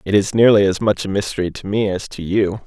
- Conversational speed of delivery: No, fast, 270 wpm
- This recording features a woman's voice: No, male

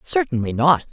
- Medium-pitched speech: Yes, medium, 150 Hz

